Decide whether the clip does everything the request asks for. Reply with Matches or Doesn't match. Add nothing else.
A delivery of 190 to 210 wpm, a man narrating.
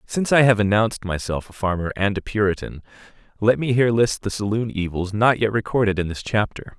Matches